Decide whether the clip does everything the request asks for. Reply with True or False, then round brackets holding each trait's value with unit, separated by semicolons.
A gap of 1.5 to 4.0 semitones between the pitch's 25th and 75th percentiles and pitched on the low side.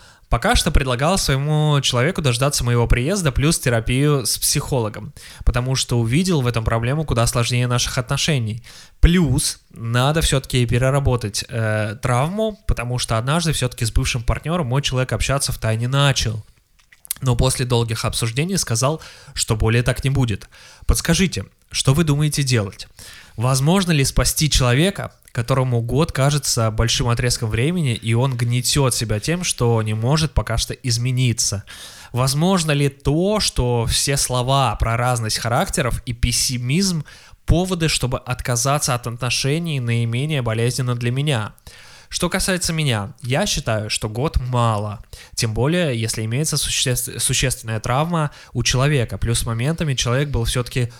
True (3.6 semitones; 125 Hz)